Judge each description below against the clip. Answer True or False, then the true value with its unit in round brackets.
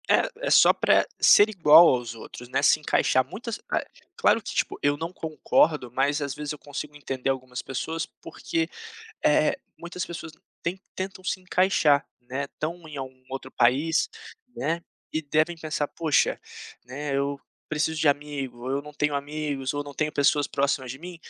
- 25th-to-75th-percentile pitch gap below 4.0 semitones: True (3.0 semitones)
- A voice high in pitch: False (145 Hz)